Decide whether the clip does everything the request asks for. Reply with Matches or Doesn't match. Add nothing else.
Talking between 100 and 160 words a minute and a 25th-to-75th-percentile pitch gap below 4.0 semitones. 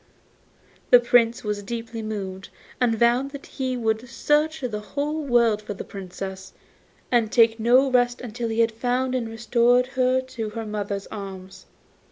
Matches